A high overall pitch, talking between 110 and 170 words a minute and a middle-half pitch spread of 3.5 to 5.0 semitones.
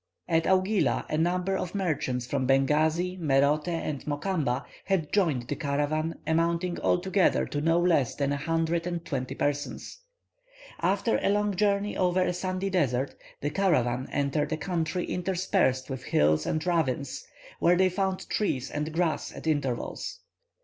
No: medium, 165 Hz; average, 150 wpm; average, 4.3 semitones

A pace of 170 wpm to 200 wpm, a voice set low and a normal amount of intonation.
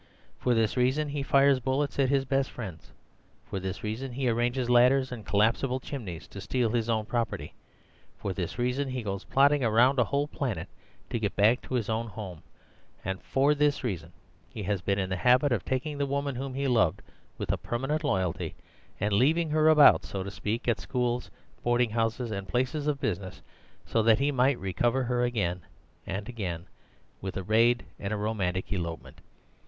Yes: average, 190 wpm; low, 120 Hz; average, 4.7 semitones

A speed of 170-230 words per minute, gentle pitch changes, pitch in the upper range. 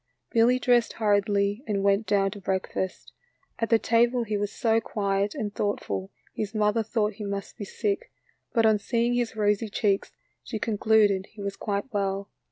Yes: average, 175 wpm; narrow, 2.2 semitones; high, 210 Hz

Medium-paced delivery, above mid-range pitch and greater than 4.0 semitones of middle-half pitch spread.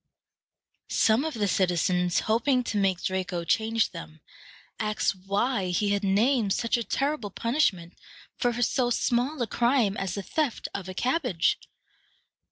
Yes: average, 145 wpm; high, 215 Hz; average, 4.5 semitones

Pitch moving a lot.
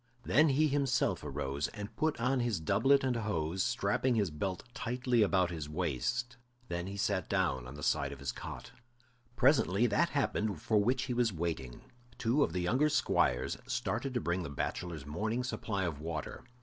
Yes: wide, 7.5 semitones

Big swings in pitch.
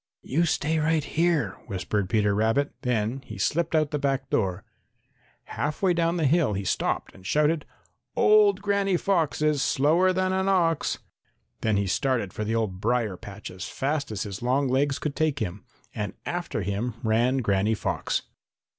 Yes: wide, 7.1 semitones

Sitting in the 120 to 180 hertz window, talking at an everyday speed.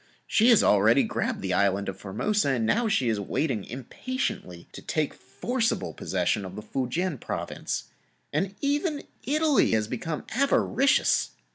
Yes: medium, 140 Hz; average, 150 wpm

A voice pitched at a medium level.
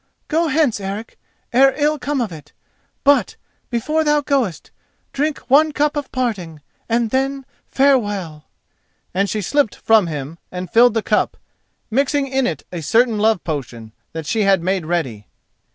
No: high, 225 Hz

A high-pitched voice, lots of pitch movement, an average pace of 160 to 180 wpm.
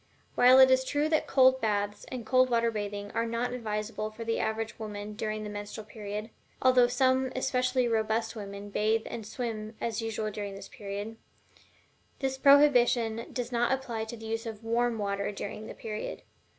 No: high, 225 Hz; average, 2.8 semitones; average, 175 wpm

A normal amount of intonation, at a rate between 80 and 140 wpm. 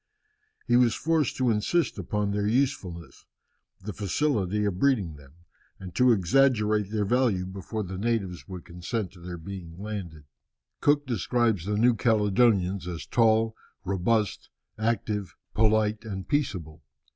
Yes: average, 4.0 semitones; slow, 135 wpm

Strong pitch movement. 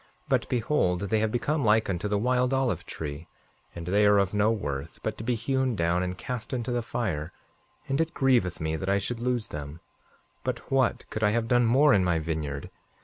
Yes: wide, 5.7 semitones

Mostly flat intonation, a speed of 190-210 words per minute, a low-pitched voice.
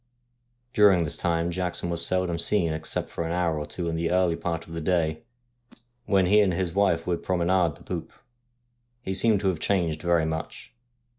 Yes: narrow, 1.9 semitones; average, 195 wpm; very low, 85 Hz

